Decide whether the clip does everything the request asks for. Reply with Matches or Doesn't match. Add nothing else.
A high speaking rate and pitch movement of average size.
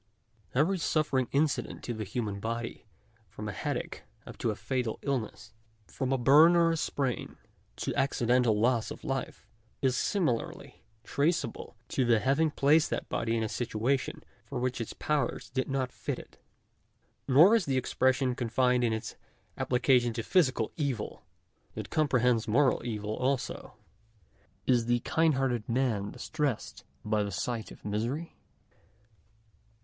Doesn't match